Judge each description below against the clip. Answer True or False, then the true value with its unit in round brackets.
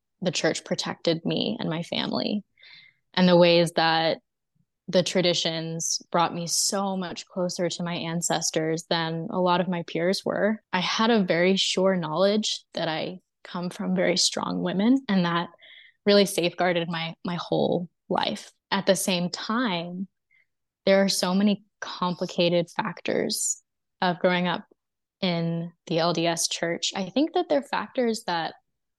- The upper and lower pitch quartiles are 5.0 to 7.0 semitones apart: False (2.5 semitones)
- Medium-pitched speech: True (180 Hz)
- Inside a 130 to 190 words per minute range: True (150 wpm)